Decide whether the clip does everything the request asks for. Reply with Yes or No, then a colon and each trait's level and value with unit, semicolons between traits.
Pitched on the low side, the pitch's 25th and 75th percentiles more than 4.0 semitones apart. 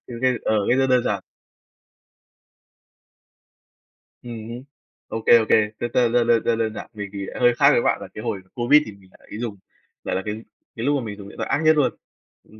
No: low, 115 Hz; average, 2.8 semitones